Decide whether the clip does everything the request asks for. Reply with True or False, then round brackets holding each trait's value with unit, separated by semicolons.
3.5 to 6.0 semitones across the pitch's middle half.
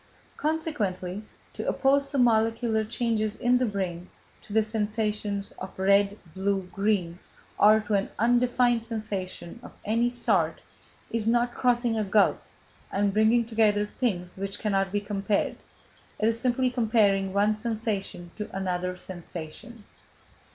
False (3.1 semitones)